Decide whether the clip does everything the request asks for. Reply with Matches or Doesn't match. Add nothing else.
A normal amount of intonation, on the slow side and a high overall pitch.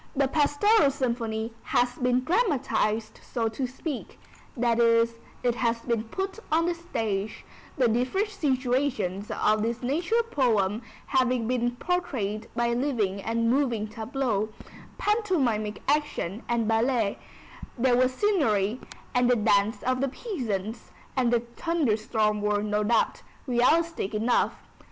Matches